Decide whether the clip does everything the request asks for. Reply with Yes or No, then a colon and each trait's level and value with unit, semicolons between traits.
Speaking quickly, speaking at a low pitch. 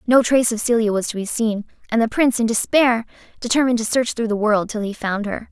No: fast, 250 wpm; high, 230 Hz